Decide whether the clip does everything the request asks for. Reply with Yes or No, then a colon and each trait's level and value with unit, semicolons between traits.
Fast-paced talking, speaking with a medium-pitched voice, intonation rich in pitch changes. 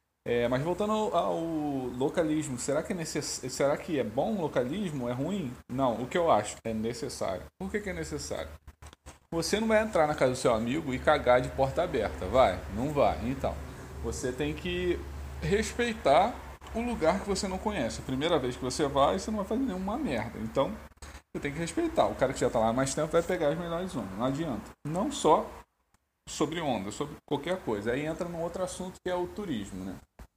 Yes: fast, 215 wpm; medium, 155 Hz; wide, 6.7 semitones